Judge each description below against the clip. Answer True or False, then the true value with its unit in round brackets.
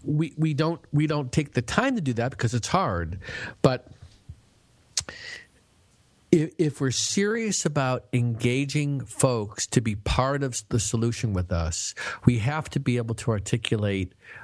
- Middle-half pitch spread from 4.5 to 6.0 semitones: True (5.1 semitones)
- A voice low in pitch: True (125 Hz)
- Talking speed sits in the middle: True (155 wpm)